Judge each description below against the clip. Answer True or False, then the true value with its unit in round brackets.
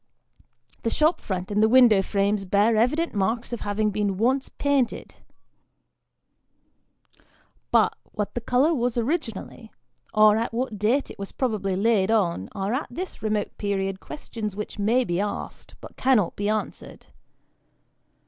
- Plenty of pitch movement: False (3.4 semitones)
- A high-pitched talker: True (215 Hz)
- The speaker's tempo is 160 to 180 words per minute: False (145 wpm)